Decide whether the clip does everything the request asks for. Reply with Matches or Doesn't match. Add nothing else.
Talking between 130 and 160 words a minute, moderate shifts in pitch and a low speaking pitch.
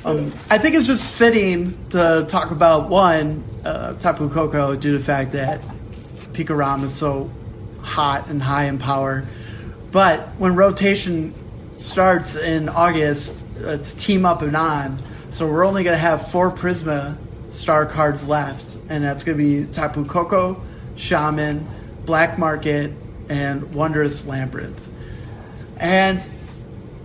Doesn't match